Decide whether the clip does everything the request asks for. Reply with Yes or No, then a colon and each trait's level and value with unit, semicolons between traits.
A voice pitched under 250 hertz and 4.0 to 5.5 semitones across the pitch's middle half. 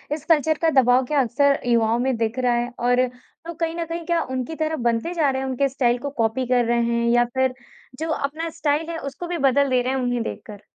No: very high, 260 Hz; average, 4.4 semitones